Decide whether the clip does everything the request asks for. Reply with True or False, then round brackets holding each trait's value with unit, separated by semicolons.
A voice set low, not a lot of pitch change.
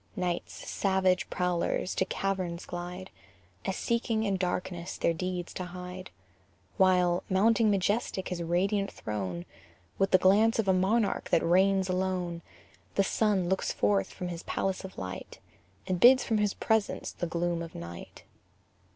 False (185 Hz; 2.0 semitones)